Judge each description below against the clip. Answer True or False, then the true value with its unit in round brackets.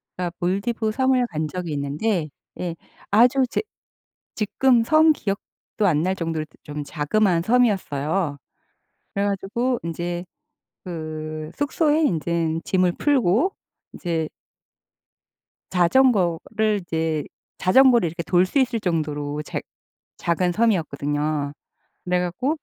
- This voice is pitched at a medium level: True (180 Hz)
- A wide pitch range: True (6.1 semitones)